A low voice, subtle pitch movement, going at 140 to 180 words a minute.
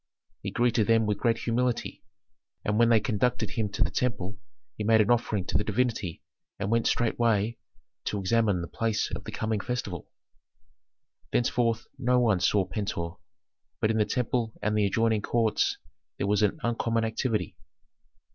Yes: low, 110 Hz; narrow, 2.1 semitones; average, 165 wpm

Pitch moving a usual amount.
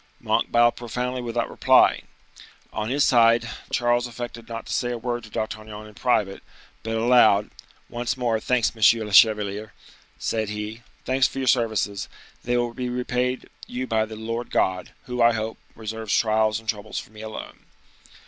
No: narrow, 2.0 semitones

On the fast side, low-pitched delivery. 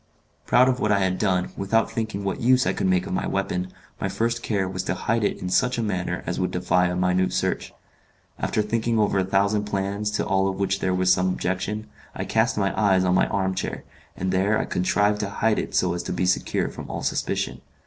Yes: fast, 235 wpm; very low, 95 Hz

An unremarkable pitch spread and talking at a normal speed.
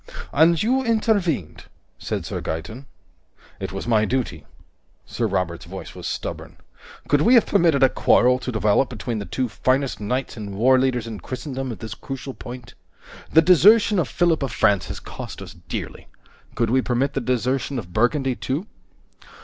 Yes: average, 4.5 semitones; average, 165 wpm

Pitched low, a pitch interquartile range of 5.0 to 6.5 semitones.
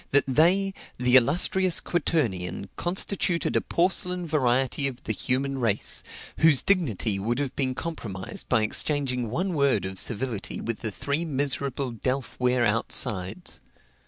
Yes: low, 130 Hz; wide, 5.4 semitones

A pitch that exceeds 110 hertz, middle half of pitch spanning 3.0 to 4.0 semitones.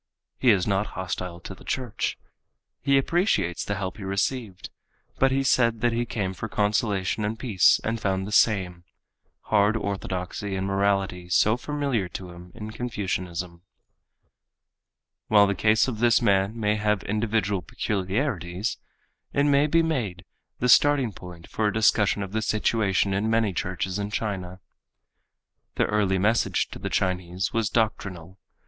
No: low, 105 Hz; average, 3.3 semitones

